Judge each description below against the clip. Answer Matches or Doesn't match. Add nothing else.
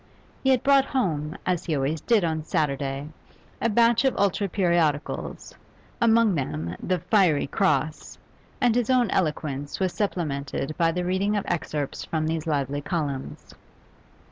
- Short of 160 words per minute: Matches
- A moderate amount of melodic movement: Doesn't match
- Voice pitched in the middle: Matches